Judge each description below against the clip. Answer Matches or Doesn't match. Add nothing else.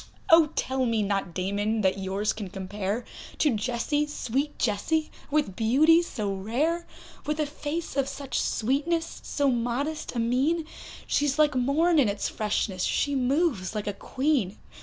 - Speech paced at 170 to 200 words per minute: Doesn't match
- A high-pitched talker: Matches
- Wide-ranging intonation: Matches